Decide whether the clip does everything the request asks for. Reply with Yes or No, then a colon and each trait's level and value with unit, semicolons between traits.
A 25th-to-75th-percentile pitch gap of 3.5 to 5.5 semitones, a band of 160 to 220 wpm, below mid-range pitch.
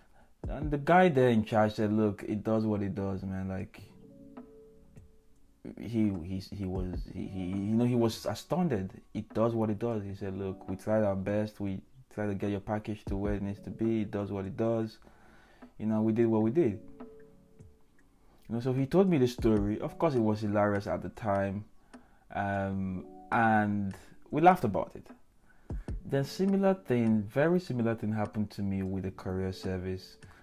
No: average, 3.0 semitones; average, 190 wpm; low, 105 Hz